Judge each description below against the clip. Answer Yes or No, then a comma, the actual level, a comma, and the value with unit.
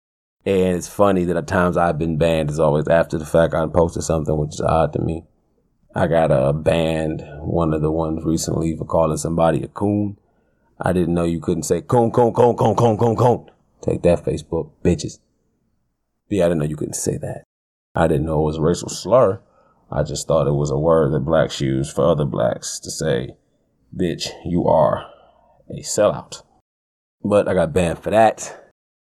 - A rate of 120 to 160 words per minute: No, average, 195 wpm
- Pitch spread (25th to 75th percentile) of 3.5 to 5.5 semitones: No, average, 2.9 semitones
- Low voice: Yes, very low, 80 Hz